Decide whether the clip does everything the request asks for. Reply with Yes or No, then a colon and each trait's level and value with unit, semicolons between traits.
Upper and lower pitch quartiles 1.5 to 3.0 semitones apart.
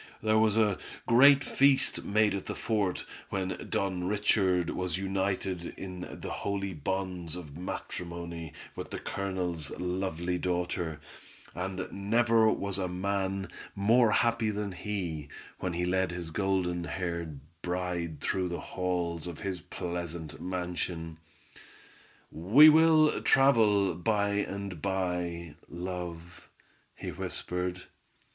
Yes: narrow, 2.4 semitones